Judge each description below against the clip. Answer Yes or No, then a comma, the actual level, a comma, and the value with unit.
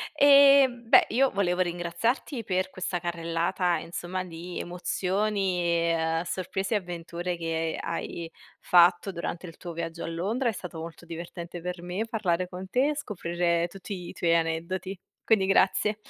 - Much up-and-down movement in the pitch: No, narrow, 2.4 semitones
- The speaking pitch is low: No, medium, 180 Hz